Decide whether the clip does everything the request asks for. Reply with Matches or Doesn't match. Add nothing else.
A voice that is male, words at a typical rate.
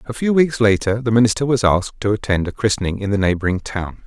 Doesn't match